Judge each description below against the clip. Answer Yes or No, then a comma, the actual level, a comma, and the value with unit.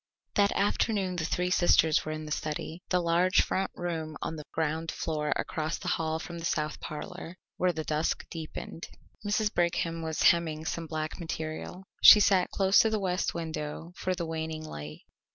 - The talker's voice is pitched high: No, medium, 165 Hz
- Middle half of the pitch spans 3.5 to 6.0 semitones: No, narrow, 2.5 semitones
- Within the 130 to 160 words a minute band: No, average, 180 wpm